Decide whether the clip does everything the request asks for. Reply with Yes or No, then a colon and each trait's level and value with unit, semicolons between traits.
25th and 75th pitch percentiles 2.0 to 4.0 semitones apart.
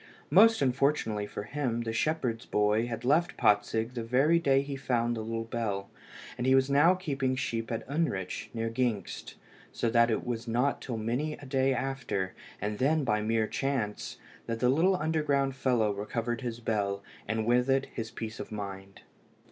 Yes: average, 3.5 semitones